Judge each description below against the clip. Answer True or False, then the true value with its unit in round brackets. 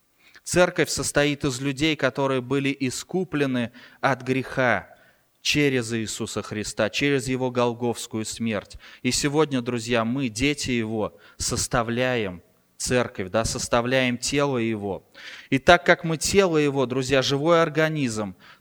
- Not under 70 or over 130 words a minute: True (120 wpm)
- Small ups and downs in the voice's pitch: False (3.5 semitones)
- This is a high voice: False (130 Hz)